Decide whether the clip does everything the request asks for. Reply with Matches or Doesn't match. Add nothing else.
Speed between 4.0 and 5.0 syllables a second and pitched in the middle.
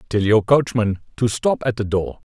Doesn't match